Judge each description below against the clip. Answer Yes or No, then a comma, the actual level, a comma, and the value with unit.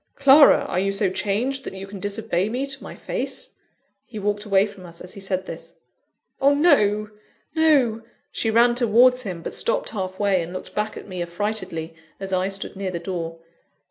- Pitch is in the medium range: No, high, 205 Hz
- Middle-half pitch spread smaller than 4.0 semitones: No, average, 4.3 semitones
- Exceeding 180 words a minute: Yes, average, 190 wpm